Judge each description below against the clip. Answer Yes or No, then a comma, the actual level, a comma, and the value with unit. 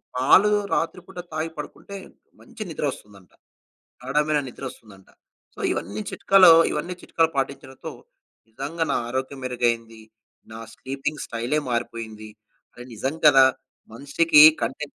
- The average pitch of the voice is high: No, low, 135 Hz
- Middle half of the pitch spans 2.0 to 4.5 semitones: No, average, 4.9 semitones